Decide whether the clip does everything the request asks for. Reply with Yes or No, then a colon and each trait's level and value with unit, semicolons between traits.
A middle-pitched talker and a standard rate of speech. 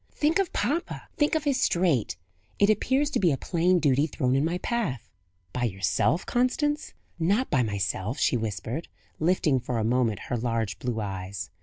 Yes: medium, 145 Hz; average, 175 wpm